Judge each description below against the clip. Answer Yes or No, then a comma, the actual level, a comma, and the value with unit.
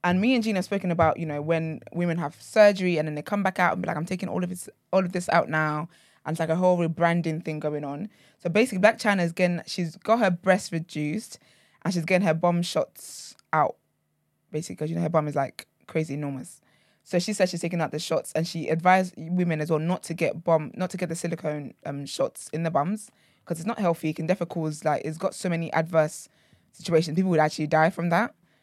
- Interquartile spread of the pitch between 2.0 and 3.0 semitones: Yes, average, 2.7 semitones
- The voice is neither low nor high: Yes, medium, 170 Hz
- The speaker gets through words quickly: Yes, fast, 245 wpm